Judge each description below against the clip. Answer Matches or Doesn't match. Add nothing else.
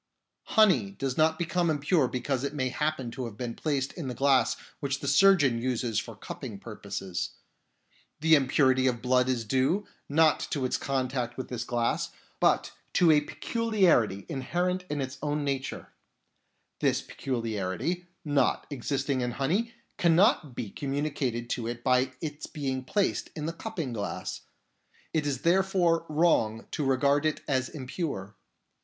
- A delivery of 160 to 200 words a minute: Doesn't match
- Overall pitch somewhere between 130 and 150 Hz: Matches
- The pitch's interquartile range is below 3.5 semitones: Doesn't match